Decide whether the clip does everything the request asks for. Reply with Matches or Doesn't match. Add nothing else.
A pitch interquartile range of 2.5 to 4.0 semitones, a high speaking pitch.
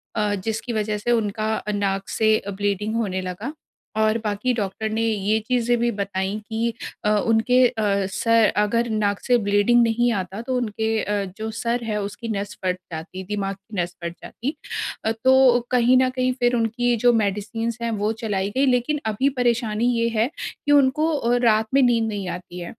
Matches